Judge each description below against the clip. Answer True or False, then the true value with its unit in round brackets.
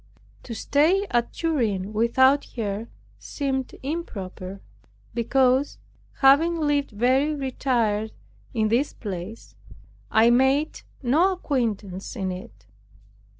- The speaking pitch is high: True (250 Hz)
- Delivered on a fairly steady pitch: False (5.0 semitones)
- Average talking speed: False (100 wpm)